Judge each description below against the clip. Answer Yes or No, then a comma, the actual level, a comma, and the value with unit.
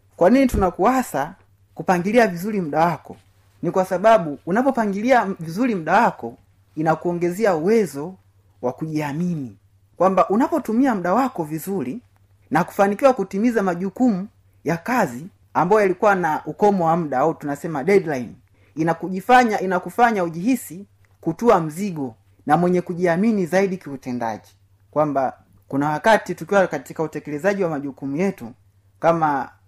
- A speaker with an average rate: Yes, average, 115 wpm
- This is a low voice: No, medium, 170 Hz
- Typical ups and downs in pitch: No, wide, 6.9 semitones